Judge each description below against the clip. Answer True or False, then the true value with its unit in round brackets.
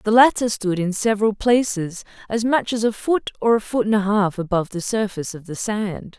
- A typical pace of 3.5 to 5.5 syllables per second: True (5.3 syllables/s)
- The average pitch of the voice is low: False (210 Hz)